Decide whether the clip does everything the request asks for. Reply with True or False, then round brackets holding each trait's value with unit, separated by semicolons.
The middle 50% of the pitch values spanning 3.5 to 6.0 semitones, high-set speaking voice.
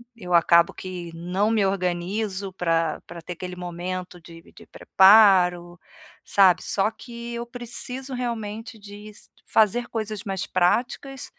True (4.0 semitones; 195 Hz)